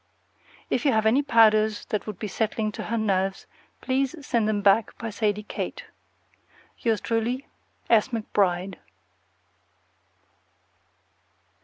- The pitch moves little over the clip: Yes, narrow, 2.0 semitones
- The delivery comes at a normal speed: No, slow, 120 wpm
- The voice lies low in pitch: No, high, 220 Hz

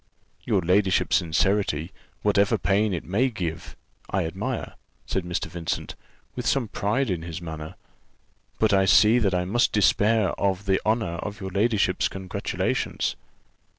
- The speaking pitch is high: No, very low, 95 Hz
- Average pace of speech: Yes, average, 150 wpm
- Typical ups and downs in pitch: Yes, average, 3.2 semitones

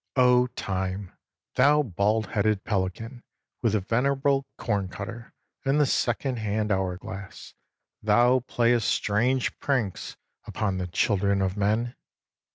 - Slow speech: Yes, slow, 115 wpm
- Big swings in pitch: No, average, 4.0 semitones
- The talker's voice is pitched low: Yes, low, 110 Hz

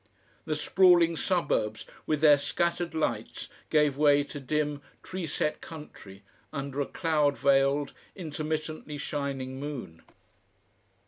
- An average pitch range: No, narrow, 2.1 semitones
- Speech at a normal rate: No, slow, 115 wpm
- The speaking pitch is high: No, medium, 150 Hz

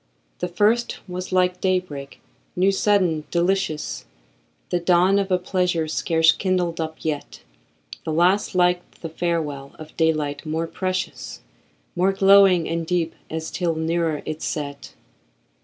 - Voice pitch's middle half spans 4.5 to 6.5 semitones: No, narrow, 2.6 semitones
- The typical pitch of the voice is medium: Yes, medium, 175 Hz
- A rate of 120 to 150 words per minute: Yes, average, 140 wpm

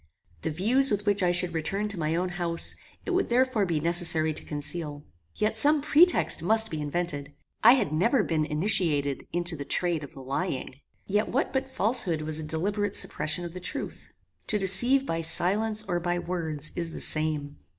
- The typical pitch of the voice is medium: Yes, medium, 175 Hz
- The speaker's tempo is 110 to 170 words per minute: No, average, 185 wpm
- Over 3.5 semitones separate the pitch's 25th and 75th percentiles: Yes, average, 5.2 semitones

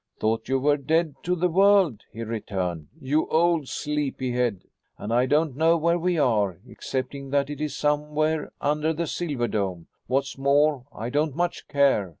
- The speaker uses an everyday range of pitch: Yes, average, 4.3 semitones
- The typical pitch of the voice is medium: Yes, medium, 145 Hz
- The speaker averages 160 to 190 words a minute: Yes, average, 170 wpm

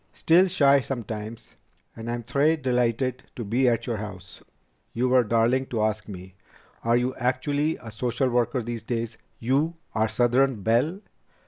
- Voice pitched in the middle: No, low, 120 Hz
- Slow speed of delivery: No, average, 155 wpm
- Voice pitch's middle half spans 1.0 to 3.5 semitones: Yes, average, 2.8 semitones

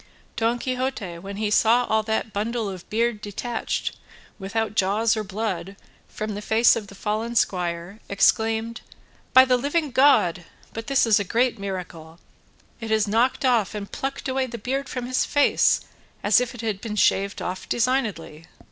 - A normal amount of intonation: Yes, average, 3.4 semitones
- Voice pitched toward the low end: No, high, 220 Hz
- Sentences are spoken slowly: No, average, 170 wpm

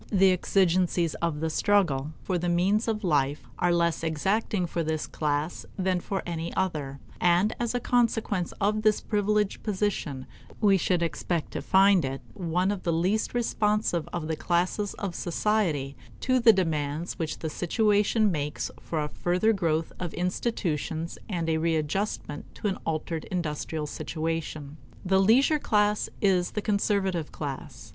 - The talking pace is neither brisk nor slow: Yes, average, 155 wpm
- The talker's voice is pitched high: No, medium, 180 Hz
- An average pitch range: Yes, average, 4.3 semitones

